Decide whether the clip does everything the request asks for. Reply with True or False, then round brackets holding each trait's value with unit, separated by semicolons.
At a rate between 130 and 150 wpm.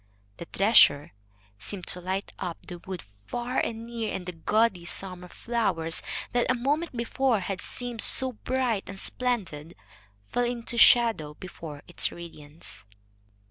True (140 wpm)